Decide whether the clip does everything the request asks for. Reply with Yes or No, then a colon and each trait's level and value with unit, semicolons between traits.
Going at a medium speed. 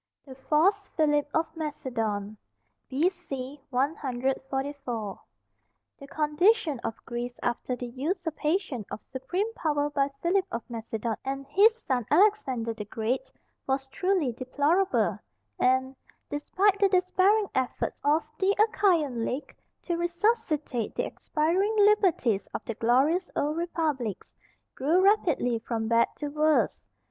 No: slow, 120 wpm